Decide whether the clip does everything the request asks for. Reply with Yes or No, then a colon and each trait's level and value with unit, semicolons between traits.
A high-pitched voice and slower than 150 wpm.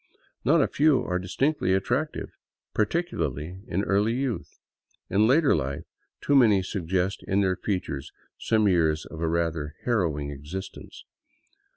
No: very low, 95 Hz; slow, 135 wpm